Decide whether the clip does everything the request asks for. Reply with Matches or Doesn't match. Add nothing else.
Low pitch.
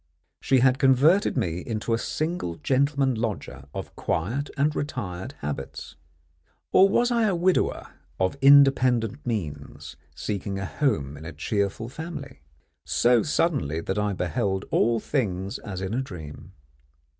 Matches